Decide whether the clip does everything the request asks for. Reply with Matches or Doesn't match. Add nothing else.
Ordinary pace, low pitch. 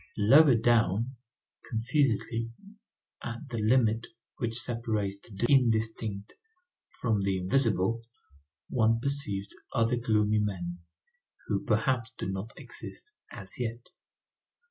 Doesn't match